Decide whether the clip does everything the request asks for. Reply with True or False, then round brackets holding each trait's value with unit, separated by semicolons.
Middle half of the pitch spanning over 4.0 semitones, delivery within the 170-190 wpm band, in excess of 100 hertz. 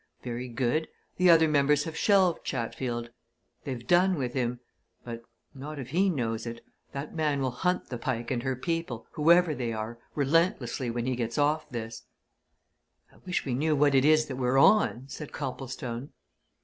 True (4.4 semitones; 175 wpm; 135 Hz)